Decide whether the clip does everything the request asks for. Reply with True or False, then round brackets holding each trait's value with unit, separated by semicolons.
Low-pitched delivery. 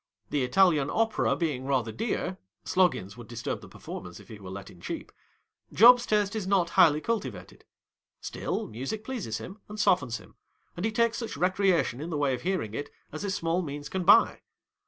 False (170 Hz)